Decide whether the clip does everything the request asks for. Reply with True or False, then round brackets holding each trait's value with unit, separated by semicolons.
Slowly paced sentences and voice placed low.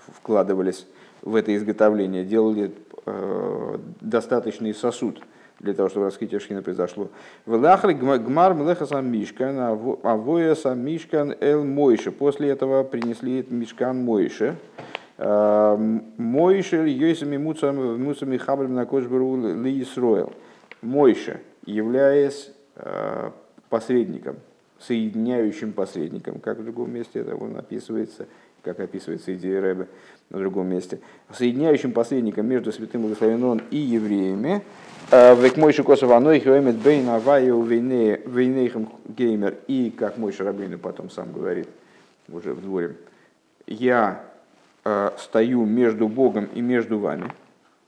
True (100 wpm; 120 Hz)